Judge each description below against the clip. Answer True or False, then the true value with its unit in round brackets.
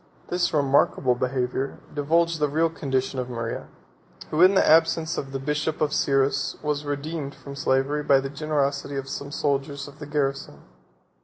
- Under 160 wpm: False (165 wpm)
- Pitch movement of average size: False (2.0 semitones)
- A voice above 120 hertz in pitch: True (140 Hz)